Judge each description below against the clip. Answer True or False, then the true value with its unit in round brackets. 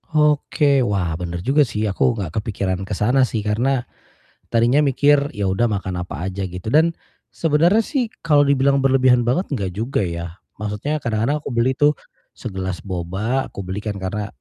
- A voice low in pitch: True (115 Hz)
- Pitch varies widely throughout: True (6.2 semitones)